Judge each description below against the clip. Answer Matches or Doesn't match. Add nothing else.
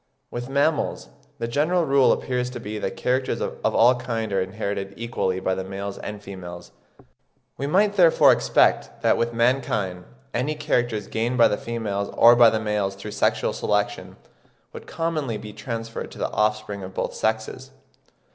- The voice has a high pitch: Doesn't match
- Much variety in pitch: Doesn't match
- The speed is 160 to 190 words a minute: Matches